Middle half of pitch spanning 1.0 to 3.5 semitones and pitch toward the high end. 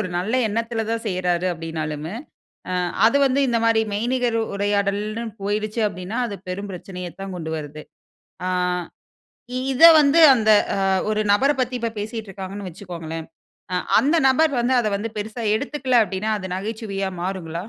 No: average, 4.0 semitones; high, 205 Hz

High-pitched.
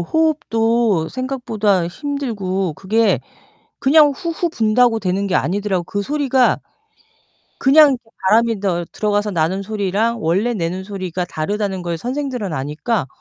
Yes: high, 210 Hz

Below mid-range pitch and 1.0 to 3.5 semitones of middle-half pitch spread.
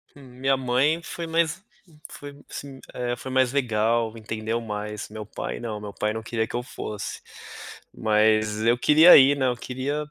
No: low, 120 Hz; average, 3.9 semitones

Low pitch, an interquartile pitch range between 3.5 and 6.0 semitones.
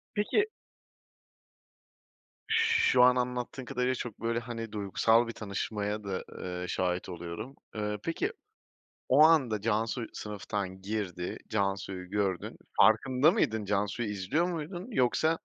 Yes: low, 110 Hz; average, 4.2 semitones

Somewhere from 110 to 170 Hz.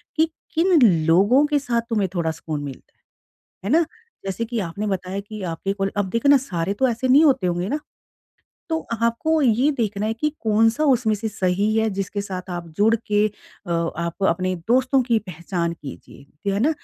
No: high, 210 Hz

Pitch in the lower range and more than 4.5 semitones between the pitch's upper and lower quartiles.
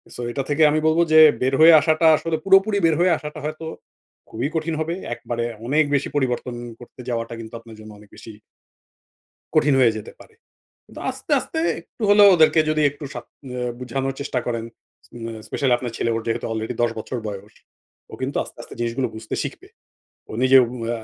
Yes: low, 130 Hz; average, 5.2 semitones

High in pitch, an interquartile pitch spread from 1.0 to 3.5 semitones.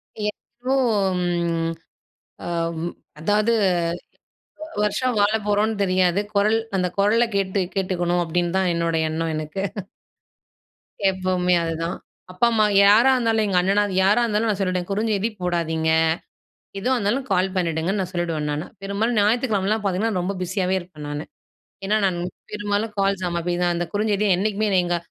Yes: high, 195 Hz; average, 3.2 semitones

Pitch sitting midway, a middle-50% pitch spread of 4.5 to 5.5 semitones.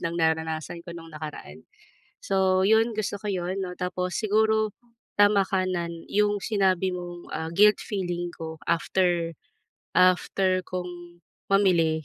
No: medium, 180 Hz; average, 2.7 semitones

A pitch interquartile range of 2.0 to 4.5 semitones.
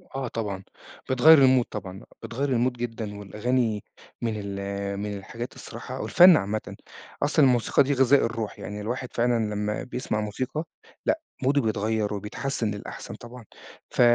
Yes: average, 3.5 semitones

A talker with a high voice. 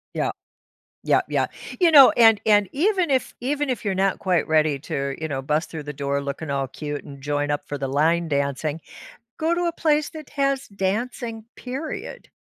No: medium, 180 Hz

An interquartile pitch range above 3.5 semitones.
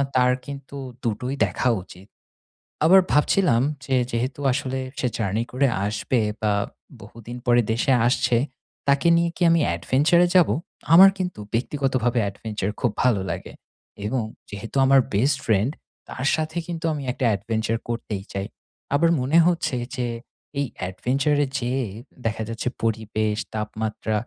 Yes: average, 4.3 semitones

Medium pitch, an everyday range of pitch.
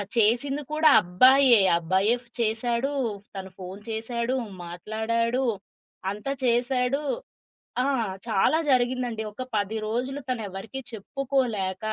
No: high, 235 Hz; average, 3.6 semitones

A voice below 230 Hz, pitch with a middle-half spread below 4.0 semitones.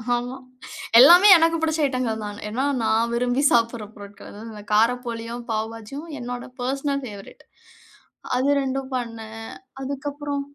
No: high, 245 Hz; average, 3.6 semitones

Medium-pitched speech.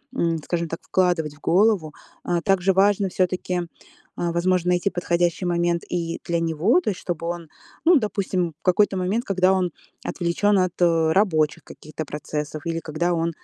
Yes: medium, 175 Hz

